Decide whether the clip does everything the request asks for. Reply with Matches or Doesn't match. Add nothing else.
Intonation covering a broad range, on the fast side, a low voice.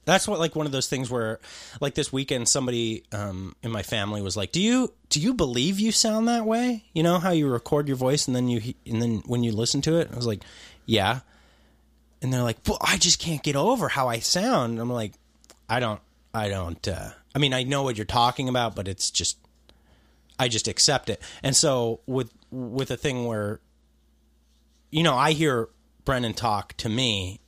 Matches